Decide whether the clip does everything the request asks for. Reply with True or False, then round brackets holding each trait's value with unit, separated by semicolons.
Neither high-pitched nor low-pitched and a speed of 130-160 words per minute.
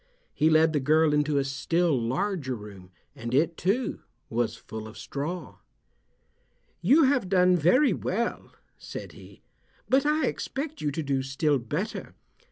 True (155 Hz; 150 wpm)